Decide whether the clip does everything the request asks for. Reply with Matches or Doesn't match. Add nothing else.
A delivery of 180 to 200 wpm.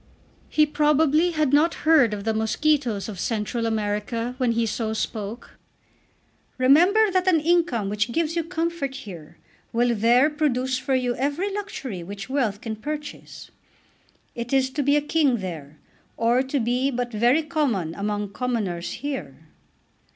Doesn't match